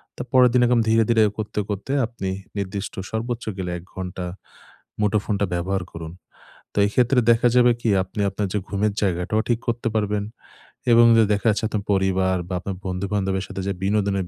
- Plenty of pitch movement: No, average, 3.0 semitones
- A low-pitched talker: Yes, low, 105 Hz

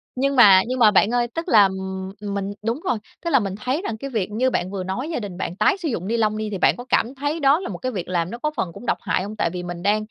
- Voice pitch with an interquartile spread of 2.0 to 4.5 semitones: No, average, 5.1 semitones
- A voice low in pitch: No, high, 215 Hz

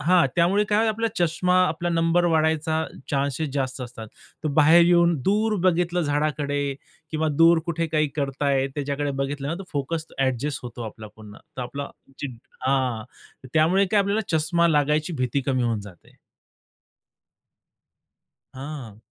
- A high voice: No, medium, 150 Hz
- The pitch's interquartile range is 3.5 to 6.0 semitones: Yes, average, 3.8 semitones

